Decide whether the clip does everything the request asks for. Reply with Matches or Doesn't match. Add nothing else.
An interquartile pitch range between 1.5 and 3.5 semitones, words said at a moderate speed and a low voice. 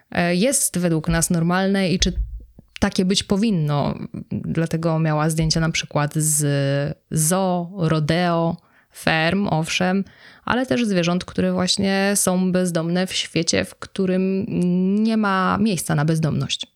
Doesn't match